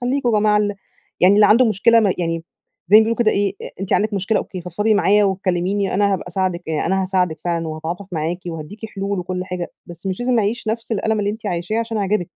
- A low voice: No, high, 195 Hz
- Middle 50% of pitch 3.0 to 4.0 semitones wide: Yes, average, 3.3 semitones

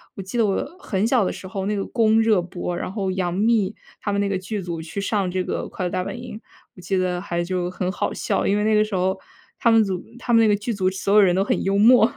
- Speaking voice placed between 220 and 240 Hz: No, high, 195 Hz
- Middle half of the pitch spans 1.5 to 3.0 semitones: Yes, narrow, 2.6 semitones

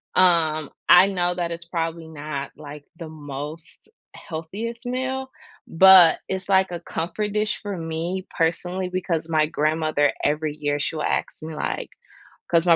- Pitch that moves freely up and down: No, average, 3.2 semitones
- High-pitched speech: No, medium, 165 Hz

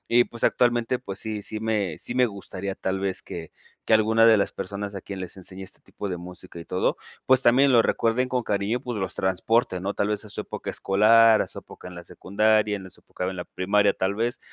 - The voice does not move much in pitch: No, average, 3.2 semitones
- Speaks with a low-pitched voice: Yes, low, 105 Hz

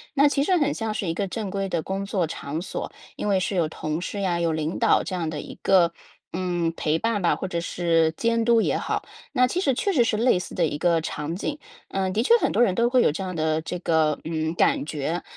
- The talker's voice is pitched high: No, medium, 180 Hz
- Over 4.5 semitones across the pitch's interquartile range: Yes, wide, 5.4 semitones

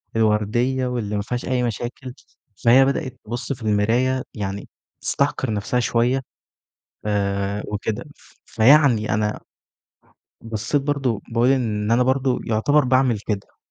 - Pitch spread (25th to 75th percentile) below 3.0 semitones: No, average, 3.6 semitones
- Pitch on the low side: Yes, low, 120 Hz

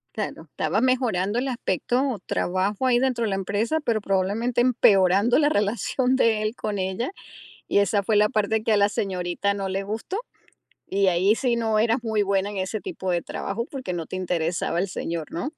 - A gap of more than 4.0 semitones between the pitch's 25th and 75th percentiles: No, average, 3.7 semitones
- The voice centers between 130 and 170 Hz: No, high, 205 Hz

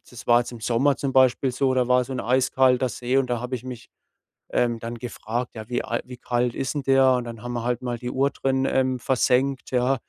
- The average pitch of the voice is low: Yes, low, 125 Hz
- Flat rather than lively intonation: Yes, narrow, 1.5 semitones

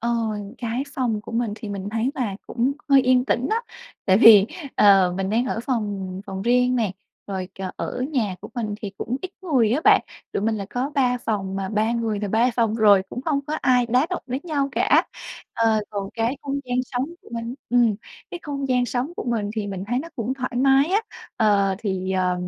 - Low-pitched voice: No, high, 230 Hz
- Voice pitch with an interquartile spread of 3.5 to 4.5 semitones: Yes, average, 3.9 semitones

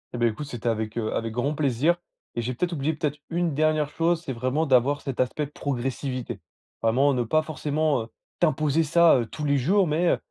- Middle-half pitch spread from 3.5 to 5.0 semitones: Yes, average, 4.0 semitones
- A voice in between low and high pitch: Yes, medium, 145 Hz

